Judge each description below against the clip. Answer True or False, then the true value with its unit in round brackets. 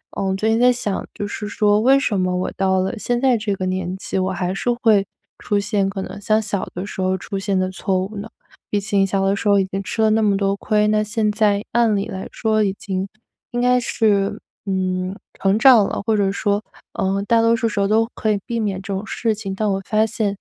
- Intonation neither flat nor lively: False (2.2 semitones)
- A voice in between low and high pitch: False (205 Hz)